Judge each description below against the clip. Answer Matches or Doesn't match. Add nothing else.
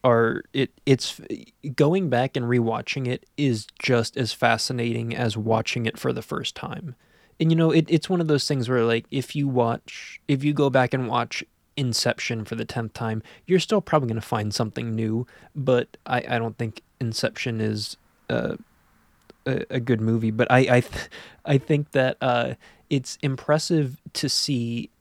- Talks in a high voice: Doesn't match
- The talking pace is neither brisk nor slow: Matches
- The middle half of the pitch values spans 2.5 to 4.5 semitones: Matches